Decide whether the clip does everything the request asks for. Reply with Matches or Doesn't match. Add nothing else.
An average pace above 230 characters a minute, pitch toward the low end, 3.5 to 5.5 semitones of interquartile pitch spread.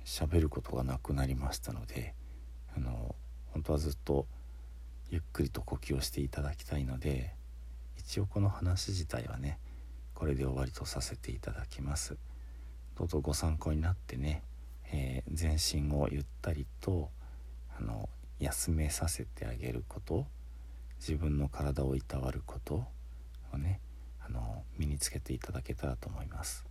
Matches